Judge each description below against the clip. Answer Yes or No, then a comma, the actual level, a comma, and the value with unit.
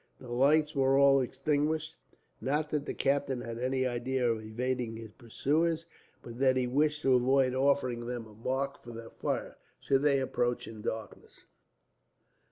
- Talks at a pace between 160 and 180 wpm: Yes, average, 170 wpm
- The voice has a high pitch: No, low, 130 Hz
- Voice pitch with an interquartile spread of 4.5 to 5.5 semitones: No, narrow, 2.6 semitones